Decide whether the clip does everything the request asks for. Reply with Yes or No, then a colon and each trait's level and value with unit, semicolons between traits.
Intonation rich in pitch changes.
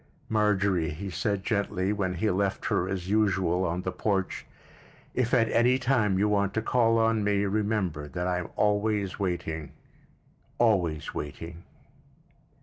No: average, 3.0 semitones